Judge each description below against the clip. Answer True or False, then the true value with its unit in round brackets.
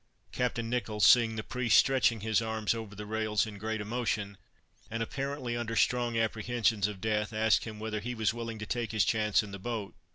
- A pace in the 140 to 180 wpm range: False (200 wpm)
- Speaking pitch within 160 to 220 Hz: False (110 Hz)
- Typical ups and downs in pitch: False (1.8 semitones)